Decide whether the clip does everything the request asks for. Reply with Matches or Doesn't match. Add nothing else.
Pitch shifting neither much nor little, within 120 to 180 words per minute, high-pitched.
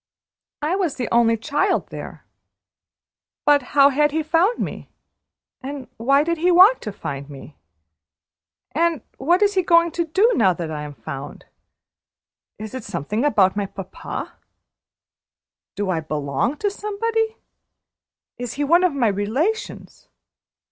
Doesn't match